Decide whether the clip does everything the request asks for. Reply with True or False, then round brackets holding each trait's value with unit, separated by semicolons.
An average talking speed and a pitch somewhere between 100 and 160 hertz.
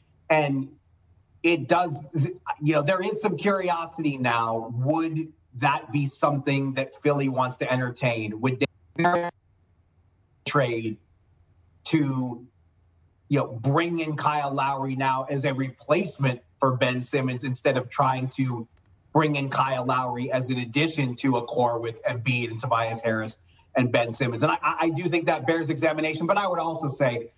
True (155 wpm; 135 Hz)